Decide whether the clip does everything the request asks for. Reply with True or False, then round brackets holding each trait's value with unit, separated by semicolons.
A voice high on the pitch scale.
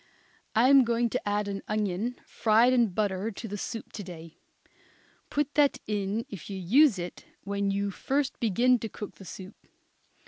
True (210 Hz)